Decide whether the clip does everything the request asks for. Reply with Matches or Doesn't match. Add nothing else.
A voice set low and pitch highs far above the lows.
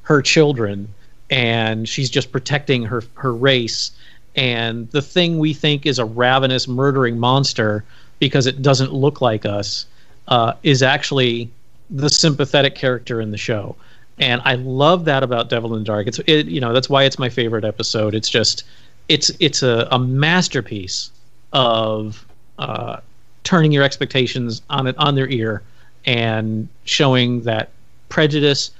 Doesn't match